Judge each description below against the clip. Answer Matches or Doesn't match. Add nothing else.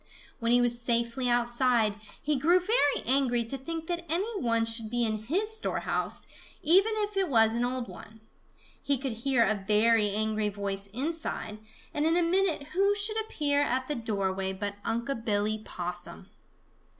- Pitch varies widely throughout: Matches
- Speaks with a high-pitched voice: Matches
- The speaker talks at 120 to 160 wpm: Doesn't match